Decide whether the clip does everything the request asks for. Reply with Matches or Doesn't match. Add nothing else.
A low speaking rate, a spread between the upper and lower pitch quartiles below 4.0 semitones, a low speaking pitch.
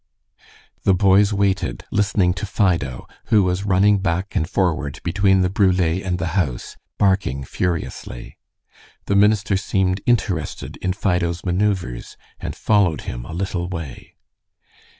Matches